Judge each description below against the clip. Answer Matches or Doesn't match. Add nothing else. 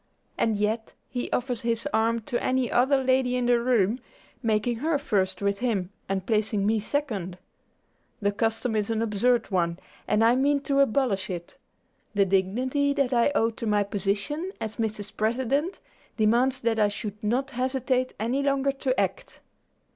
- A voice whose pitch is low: Doesn't match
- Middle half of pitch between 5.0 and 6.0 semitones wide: Doesn't match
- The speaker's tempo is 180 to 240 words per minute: Doesn't match